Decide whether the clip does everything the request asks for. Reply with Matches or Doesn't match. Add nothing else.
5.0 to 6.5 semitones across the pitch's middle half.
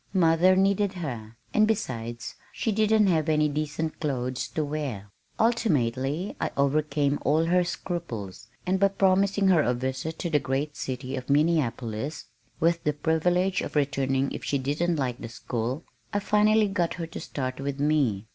Matches